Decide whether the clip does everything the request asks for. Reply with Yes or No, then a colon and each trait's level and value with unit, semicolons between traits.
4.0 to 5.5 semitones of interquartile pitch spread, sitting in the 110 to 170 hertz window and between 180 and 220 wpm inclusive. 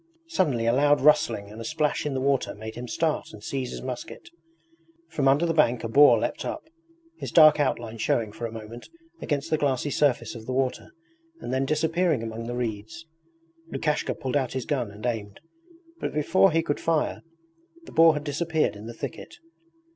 Yes: average, 4.7 semitones; low, 135 Hz; average, 190 wpm